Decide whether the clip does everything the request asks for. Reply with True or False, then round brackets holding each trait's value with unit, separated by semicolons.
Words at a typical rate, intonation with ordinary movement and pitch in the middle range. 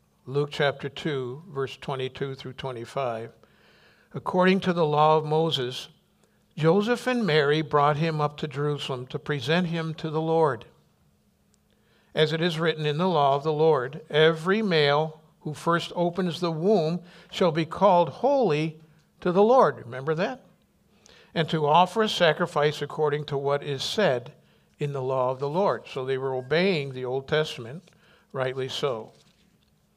True (155 wpm; 3.6 semitones; 155 Hz)